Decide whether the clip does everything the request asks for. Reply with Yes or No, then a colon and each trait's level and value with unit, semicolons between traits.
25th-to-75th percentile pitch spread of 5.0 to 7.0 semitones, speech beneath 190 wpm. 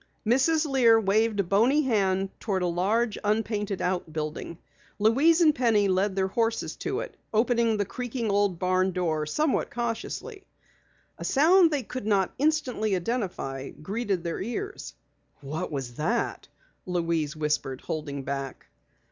Yes: wide, 5.4 semitones; average, 140 wpm